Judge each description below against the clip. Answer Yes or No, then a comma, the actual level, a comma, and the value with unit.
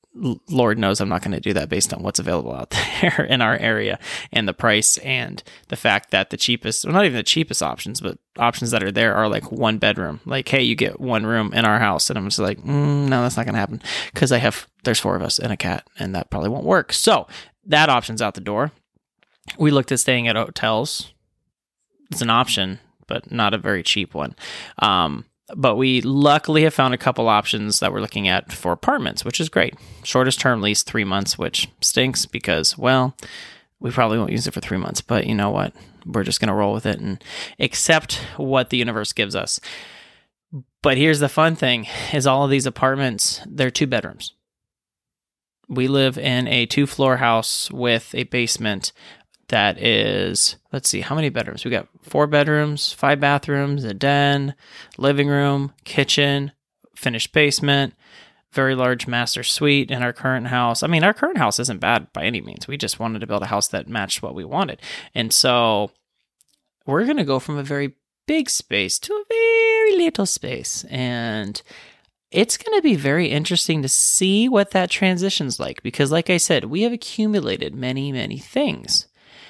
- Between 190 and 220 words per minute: Yes, average, 195 wpm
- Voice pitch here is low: Yes, low, 130 Hz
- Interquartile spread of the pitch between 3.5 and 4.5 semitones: Yes, average, 4.2 semitones